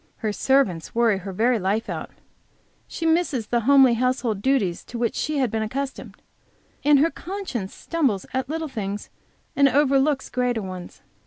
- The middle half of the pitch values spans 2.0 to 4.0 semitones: No, average, 4.6 semitones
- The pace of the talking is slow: No, average, 160 wpm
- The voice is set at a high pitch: Yes, very high, 250 Hz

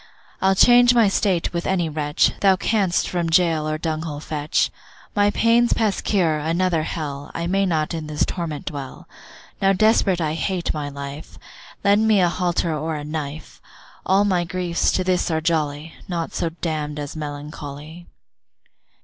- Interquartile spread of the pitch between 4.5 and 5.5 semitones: No, average, 3.5 semitones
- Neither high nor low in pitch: Yes, medium, 165 Hz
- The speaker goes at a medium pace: Yes, average, 165 wpm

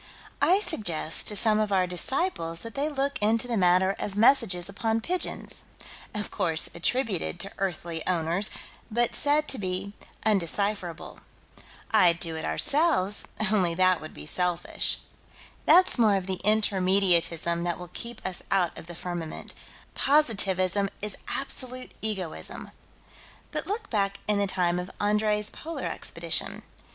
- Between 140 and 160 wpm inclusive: Yes, average, 145 wpm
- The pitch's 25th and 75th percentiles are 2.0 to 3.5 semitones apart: No, average, 4.2 semitones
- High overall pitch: Yes, high, 195 Hz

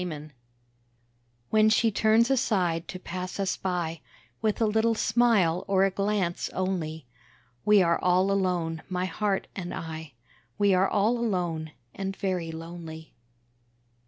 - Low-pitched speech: No, medium, 185 Hz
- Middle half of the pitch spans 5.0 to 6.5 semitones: No, average, 3.7 semitones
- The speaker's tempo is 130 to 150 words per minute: Yes, average, 140 wpm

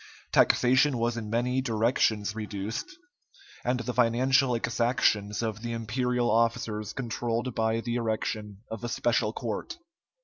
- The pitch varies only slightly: Yes, narrow, 2.0 semitones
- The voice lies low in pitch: Yes, low, 115 Hz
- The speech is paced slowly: Yes, slow, 130 wpm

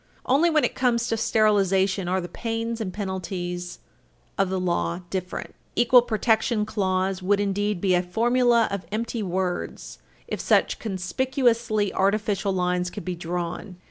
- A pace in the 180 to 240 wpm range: No, average, 150 wpm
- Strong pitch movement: No, average, 3.7 semitones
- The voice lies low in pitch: No, high, 200 Hz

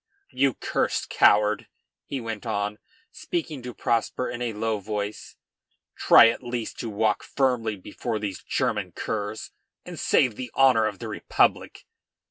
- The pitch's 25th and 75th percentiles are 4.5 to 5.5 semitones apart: No, average, 2.8 semitones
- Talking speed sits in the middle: Yes, average, 145 wpm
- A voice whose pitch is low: Yes, low, 110 Hz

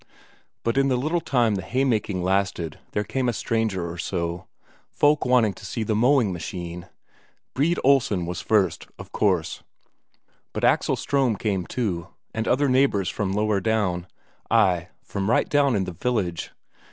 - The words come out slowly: No, average, 160 wpm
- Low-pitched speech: Yes, low, 105 Hz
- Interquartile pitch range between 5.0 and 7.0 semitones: Yes, wide, 5.5 semitones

